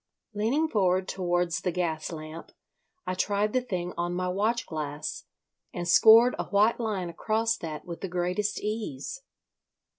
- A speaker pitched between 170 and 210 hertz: Yes, medium, 185 Hz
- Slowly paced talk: No, average, 150 wpm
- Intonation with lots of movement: No, average, 3.8 semitones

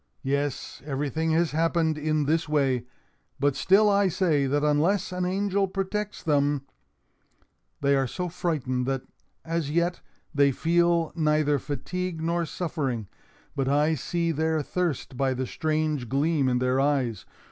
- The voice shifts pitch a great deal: No, average, 3.6 semitones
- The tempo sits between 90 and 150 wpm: Yes, average, 145 wpm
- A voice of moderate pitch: Yes, medium, 155 Hz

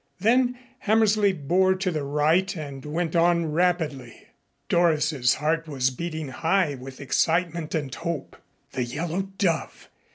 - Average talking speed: No, slow, 130 wpm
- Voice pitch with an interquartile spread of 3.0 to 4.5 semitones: Yes, average, 3.8 semitones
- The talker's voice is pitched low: No, medium, 165 Hz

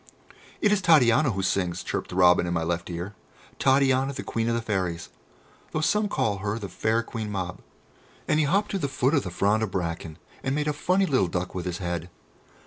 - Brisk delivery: Yes, fast, 220 wpm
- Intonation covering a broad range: Yes, wide, 7.5 semitones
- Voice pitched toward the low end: Yes, low, 105 Hz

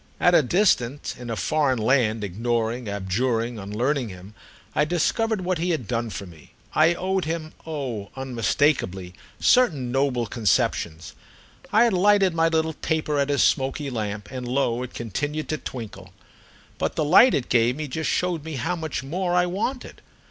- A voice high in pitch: No, low, 135 Hz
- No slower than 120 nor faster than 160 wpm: No, average, 170 wpm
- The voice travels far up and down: Yes, wide, 6.0 semitones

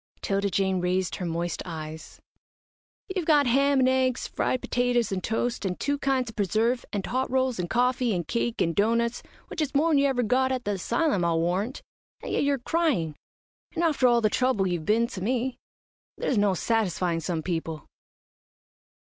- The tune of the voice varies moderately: No, wide, 5.9 semitones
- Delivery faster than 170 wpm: Yes, average, 180 wpm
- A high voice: Yes, high, 230 Hz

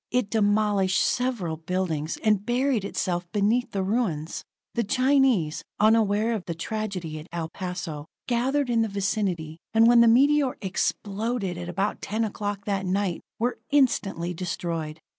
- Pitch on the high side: Yes, high, 200 Hz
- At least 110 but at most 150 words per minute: Yes, average, 145 wpm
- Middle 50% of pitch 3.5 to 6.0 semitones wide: Yes, average, 4.7 semitones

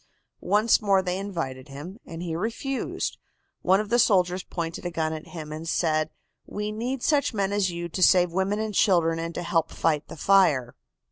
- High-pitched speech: No, medium, 180 Hz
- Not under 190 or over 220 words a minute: Yes, average, 195 wpm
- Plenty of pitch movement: No, average, 3.7 semitones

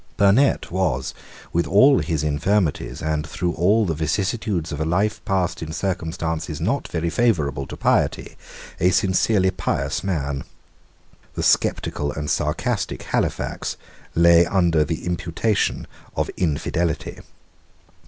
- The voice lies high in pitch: No, very low, 85 Hz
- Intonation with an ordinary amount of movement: Yes, average, 3.9 semitones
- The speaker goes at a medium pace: No, slow, 125 wpm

